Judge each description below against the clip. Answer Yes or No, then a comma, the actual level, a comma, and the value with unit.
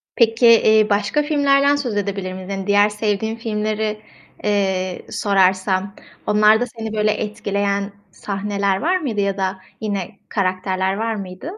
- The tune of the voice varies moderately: No, narrow, 2.1 semitones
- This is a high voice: Yes, high, 205 Hz